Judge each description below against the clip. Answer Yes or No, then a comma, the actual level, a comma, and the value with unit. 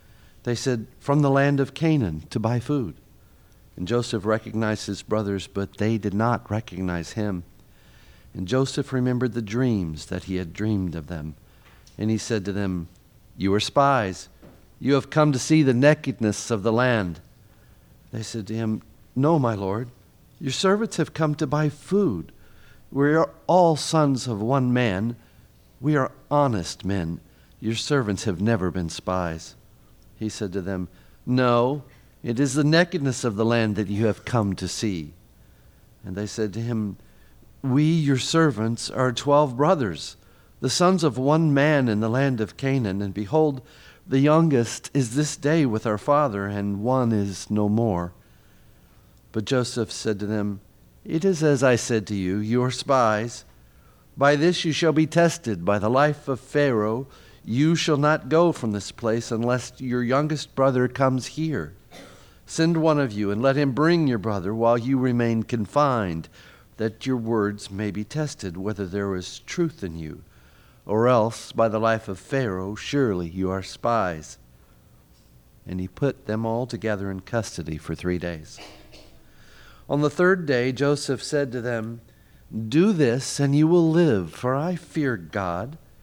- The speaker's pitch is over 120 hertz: No, low, 115 Hz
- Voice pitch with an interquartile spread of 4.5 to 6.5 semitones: Yes, wide, 5.6 semitones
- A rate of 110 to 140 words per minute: No, average, 165 wpm